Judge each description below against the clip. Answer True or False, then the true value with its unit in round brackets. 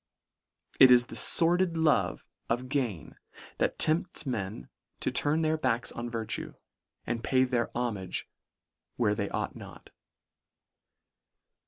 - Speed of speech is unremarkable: False (125 wpm)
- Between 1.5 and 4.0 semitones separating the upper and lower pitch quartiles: False (5.0 semitones)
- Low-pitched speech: True (125 Hz)